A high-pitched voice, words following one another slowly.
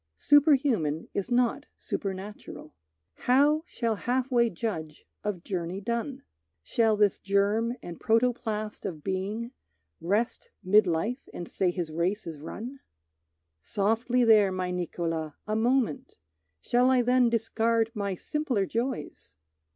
Yes: high, 215 Hz; slow, 125 wpm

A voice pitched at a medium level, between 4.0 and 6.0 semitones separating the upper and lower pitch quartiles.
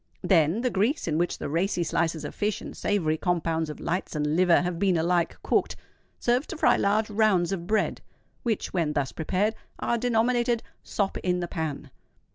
Yes: medium, 180 Hz; average, 4.7 semitones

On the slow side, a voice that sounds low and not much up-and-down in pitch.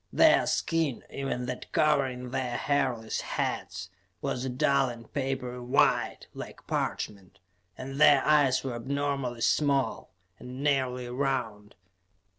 Yes: slow, 120 wpm; low, 130 Hz; narrow, 2.1 semitones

